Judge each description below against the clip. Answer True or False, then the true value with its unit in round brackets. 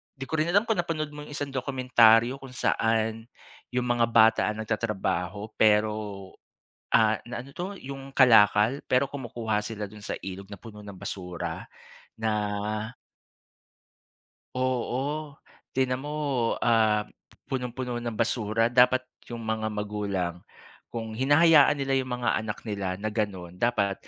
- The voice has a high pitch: False (115 Hz)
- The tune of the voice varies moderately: True (3.7 semitones)